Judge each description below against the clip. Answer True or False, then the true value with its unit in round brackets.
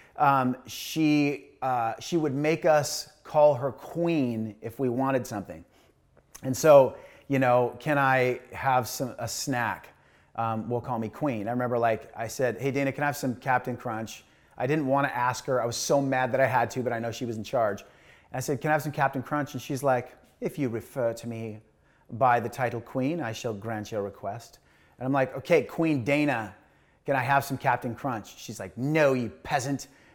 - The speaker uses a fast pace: True (210 wpm)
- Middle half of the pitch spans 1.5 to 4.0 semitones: True (3.3 semitones)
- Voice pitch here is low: True (130 Hz)